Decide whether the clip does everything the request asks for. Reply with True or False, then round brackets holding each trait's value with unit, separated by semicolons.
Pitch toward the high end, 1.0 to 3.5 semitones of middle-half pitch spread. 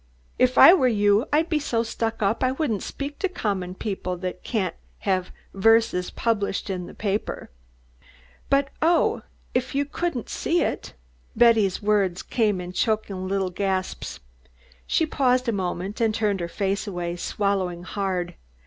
False (205 Hz; 4.8 semitones)